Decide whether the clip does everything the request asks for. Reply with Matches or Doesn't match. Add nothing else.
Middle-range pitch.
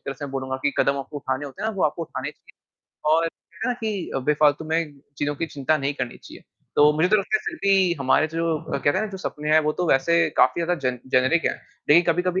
Matches